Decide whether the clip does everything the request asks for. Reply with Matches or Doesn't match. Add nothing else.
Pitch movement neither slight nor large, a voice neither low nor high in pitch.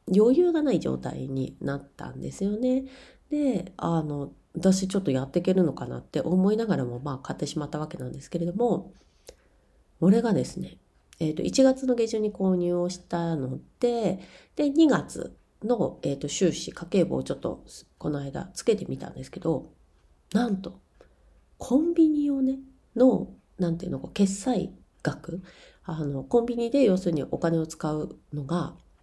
Doesn't match